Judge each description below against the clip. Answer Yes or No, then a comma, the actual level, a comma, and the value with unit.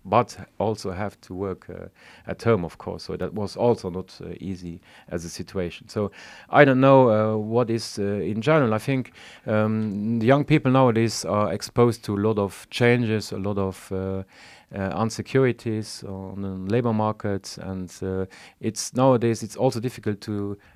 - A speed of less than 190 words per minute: Yes, average, 180 wpm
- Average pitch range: Yes, average, 3.4 semitones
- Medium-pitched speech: No, low, 110 Hz